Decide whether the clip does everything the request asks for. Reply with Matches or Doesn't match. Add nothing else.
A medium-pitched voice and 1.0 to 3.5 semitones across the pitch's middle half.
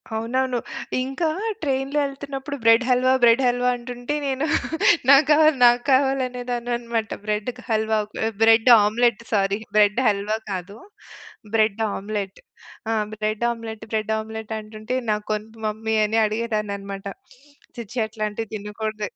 Doesn't match